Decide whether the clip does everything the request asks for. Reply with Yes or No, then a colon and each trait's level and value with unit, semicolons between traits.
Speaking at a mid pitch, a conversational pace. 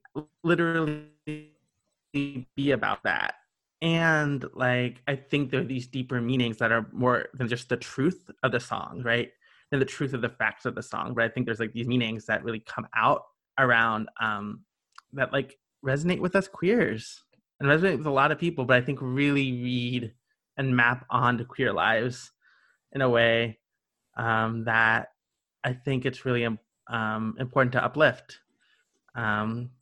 No: low, 125 Hz; average, 165 wpm